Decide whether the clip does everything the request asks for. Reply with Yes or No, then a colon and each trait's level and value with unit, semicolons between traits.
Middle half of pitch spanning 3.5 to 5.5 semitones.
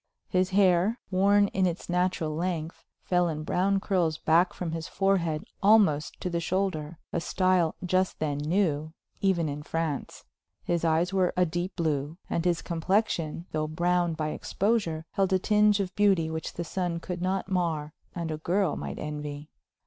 No: average, 3.0 semitones